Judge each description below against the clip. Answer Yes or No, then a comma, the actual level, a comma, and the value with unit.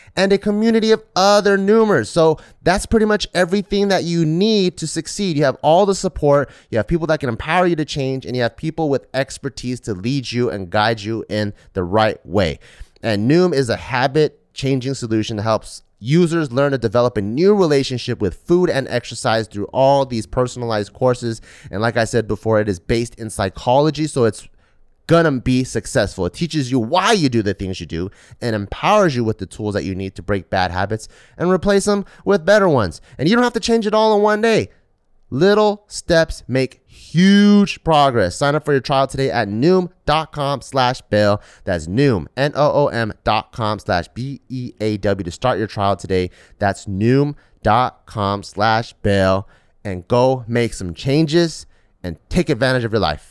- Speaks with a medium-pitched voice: No, low, 125 Hz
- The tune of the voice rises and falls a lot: Yes, wide, 7.4 semitones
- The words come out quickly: No, average, 190 wpm